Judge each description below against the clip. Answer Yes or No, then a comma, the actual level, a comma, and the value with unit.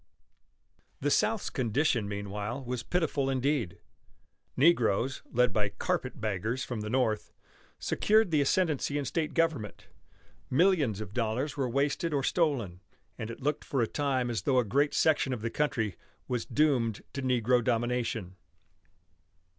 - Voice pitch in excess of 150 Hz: No, low, 125 Hz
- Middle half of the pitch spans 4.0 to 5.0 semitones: Yes, average, 4.6 semitones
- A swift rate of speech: No, average, 145 wpm